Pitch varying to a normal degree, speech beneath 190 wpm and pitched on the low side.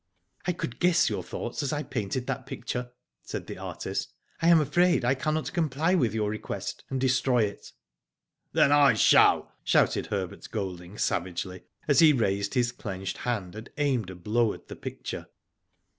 No: wide, 6.2 semitones; average, 175 wpm; low, 125 Hz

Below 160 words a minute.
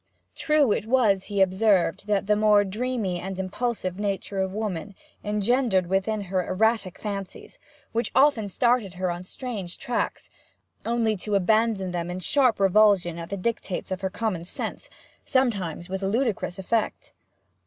Yes: average, 150 wpm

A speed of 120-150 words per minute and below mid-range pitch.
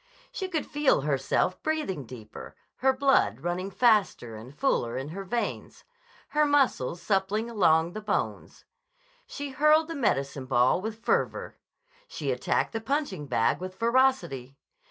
No: average, 145 wpm; high, 195 Hz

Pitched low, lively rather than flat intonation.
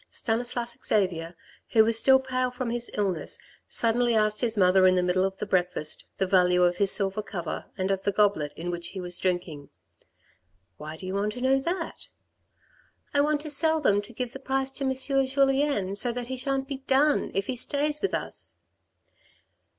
No: high, 220 Hz; wide, 6.2 semitones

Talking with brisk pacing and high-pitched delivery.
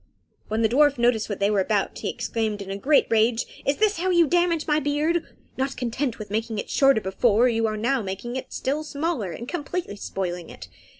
Yes: fast, 215 wpm; high, 240 Hz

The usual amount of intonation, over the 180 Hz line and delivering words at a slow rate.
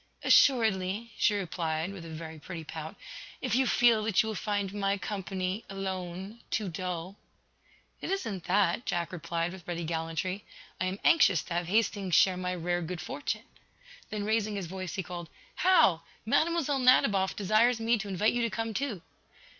No: average, 3.8 semitones; high, 190 Hz; average, 170 wpm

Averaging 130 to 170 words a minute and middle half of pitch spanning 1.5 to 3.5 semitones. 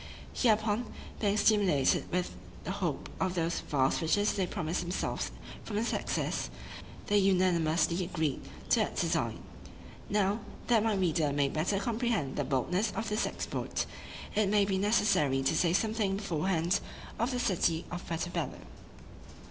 No: average, 150 wpm; average, 4.1 semitones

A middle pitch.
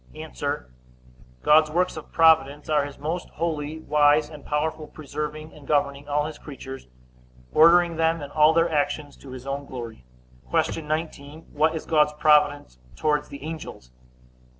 Yes: medium, 150 Hz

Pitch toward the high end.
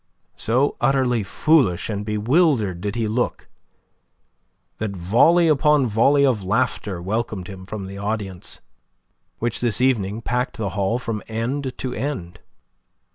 No: low, 110 Hz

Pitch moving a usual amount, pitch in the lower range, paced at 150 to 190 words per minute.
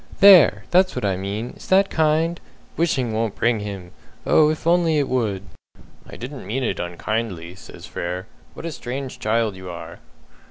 No: wide, 8.1 semitones; low, 115 Hz; average, 170 wpm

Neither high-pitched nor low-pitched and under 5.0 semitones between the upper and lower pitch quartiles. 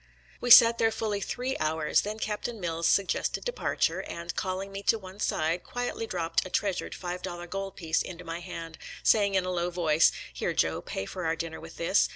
Yes: medium, 180 Hz; average, 3.5 semitones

